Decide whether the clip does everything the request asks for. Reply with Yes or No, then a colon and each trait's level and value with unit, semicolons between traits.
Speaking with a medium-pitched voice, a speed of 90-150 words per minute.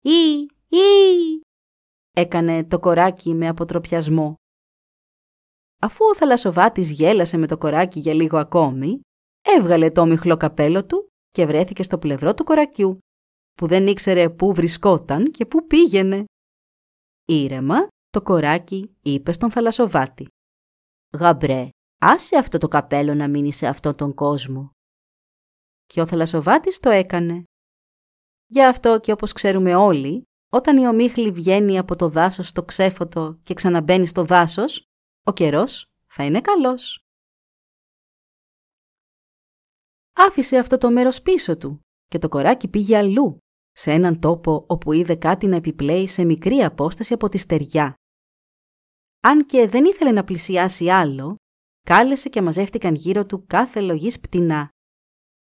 Yes: medium, 180 Hz; average, 130 wpm